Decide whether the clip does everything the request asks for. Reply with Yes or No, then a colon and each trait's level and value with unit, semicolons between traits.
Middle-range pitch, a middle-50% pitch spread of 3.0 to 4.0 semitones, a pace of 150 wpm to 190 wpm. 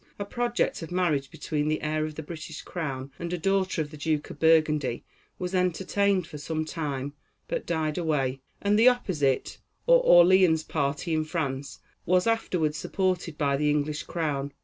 Yes: medium, 160 Hz; average, 3.6 semitones; average, 170 wpm